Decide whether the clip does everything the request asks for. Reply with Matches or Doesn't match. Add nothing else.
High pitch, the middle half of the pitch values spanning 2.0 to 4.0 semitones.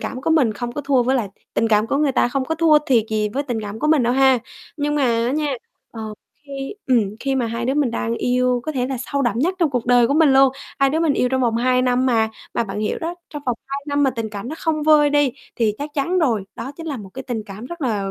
Matches